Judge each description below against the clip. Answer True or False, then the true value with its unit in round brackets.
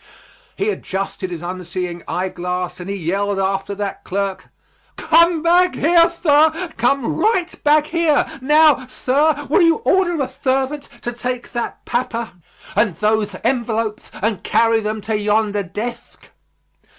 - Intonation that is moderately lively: False (7.4 semitones)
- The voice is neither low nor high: False (235 Hz)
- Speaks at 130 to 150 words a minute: True (140 wpm)